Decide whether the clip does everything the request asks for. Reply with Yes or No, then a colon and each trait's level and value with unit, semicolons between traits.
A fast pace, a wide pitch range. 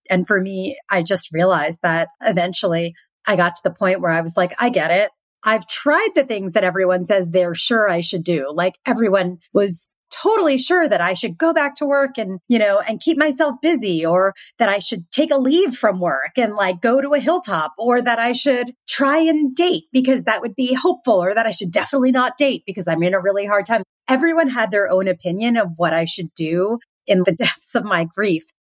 Yes: fast, 225 wpm; wide, 6.9 semitones